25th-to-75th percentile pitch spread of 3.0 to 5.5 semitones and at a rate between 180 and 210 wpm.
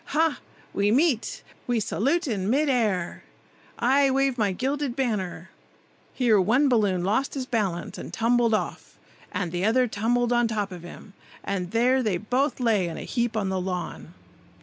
No: average, 4.9 semitones; average, 170 wpm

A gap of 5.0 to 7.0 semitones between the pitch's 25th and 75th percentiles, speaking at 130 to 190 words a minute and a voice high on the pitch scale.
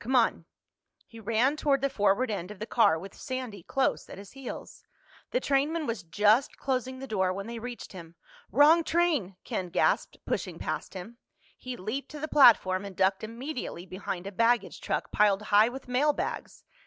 Yes: wide, 5.4 semitones; average, 180 wpm; high, 230 Hz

